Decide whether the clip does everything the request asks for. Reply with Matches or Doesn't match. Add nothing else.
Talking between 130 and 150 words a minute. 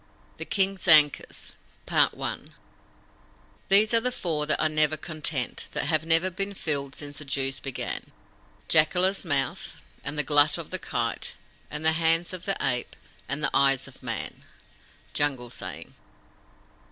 Matches